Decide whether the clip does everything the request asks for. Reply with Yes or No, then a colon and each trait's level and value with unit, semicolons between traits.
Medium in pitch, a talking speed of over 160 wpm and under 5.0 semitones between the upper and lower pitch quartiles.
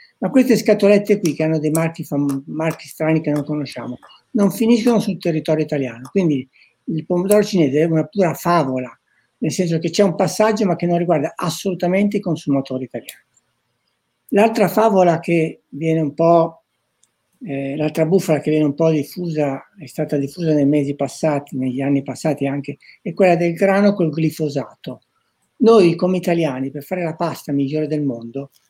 Yes: medium, 160 Hz; fast, 170 wpm; average, 4.1 semitones